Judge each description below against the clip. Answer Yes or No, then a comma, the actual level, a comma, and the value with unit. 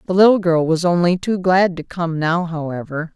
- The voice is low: No, medium, 170 Hz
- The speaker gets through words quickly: Yes, fast, 210 wpm